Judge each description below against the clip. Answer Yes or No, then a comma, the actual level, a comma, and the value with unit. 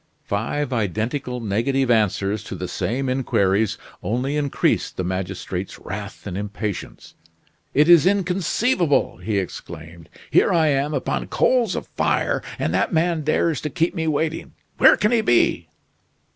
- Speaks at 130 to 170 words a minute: Yes, average, 145 wpm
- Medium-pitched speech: No, low, 130 Hz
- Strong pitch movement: Yes, wide, 7.8 semitones